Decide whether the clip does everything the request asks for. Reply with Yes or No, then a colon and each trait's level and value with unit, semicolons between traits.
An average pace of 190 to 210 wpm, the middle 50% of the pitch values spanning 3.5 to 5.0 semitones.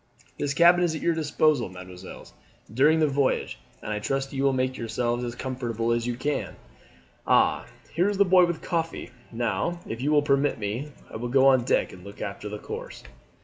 Yes: average, 200 wpm; average, 4.7 semitones